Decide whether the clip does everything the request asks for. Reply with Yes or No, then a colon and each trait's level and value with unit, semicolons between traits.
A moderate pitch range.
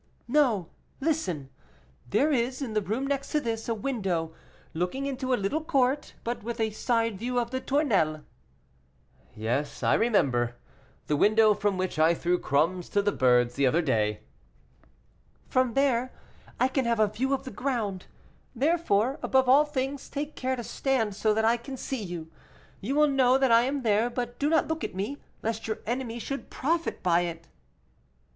No: wide, 6.0 semitones